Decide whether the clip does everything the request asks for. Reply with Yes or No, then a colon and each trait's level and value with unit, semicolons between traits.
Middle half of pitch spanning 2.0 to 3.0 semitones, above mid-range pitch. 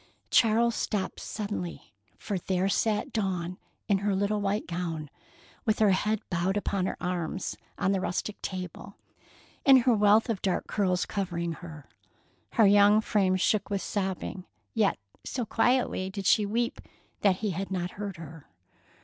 Yes: narrow, 2.6 semitones; high, 195 Hz